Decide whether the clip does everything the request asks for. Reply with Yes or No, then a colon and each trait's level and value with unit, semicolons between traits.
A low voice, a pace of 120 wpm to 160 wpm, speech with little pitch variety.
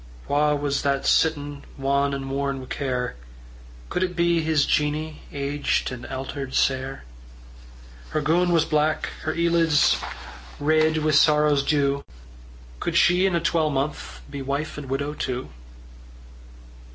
No: medium, 145 Hz; average, 140 wpm; narrow, 2.2 semitones